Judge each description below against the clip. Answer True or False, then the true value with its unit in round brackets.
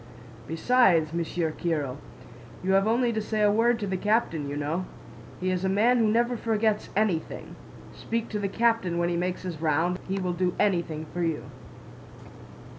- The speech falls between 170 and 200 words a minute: True (180 wpm)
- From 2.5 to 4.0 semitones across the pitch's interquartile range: False (4.4 semitones)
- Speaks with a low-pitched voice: False (185 Hz)